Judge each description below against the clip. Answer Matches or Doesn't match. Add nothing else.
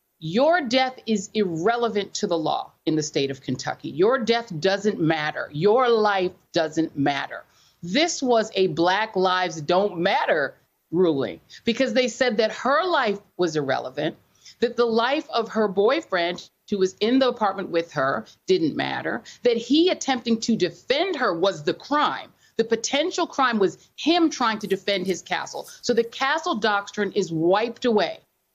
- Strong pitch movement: Matches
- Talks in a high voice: Matches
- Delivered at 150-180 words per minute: Matches